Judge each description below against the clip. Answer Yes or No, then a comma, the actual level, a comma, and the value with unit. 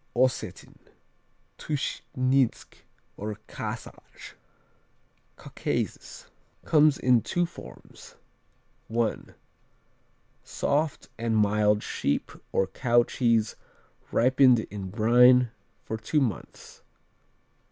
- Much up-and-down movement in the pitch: No, average, 3.4 semitones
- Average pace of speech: No, slow, 80 wpm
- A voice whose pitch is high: No, low, 120 Hz